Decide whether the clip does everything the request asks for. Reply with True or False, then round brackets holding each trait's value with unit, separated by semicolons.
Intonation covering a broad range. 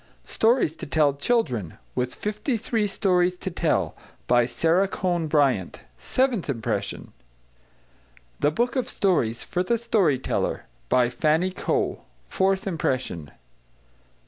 True (7.7 semitones)